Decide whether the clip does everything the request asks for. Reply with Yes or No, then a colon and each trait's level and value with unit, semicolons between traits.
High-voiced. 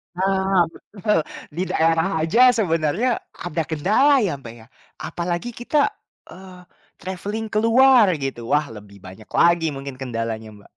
No: medium, 175 Hz